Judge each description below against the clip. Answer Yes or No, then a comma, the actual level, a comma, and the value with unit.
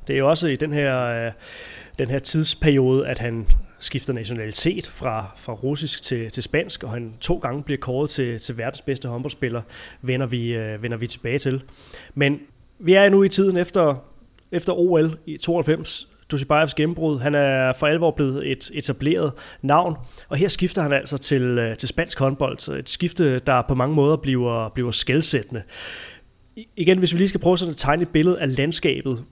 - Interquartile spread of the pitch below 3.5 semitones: No, average, 4.1 semitones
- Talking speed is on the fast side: No, average, 180 wpm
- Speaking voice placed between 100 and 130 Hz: No, medium, 140 Hz